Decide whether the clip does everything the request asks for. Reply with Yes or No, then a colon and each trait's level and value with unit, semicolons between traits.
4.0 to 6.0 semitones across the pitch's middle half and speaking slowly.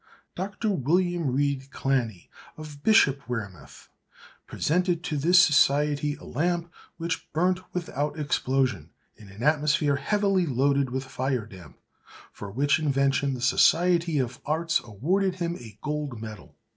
Yes: average, 4.6 semitones; slow, 130 wpm